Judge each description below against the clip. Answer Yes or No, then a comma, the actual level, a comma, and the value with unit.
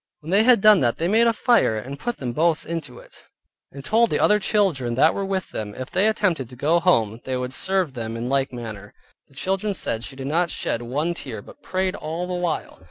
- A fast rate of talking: Yes, fast, 240 wpm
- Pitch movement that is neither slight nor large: No, wide, 7.2 semitones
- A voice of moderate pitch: Yes, medium, 160 Hz